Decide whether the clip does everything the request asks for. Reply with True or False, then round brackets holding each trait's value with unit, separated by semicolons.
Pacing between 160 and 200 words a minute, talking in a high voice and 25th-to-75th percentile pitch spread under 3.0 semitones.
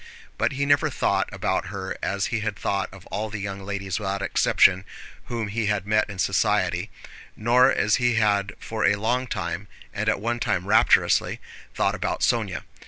False (180 wpm; 105 Hz; 2.4 semitones)